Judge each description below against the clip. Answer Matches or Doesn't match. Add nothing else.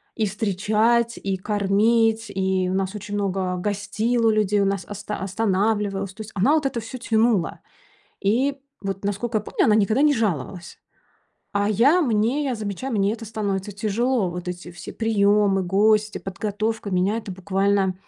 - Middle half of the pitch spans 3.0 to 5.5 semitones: Doesn't match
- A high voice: Matches